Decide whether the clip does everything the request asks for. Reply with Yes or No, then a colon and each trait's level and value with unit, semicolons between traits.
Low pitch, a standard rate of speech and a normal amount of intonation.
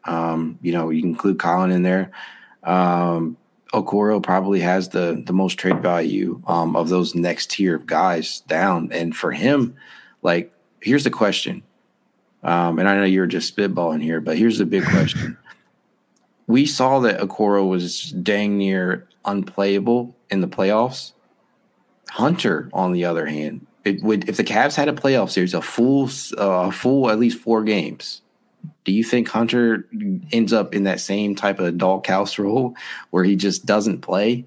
Yes: low, 100 Hz; average, 170 wpm; average, 3.9 semitones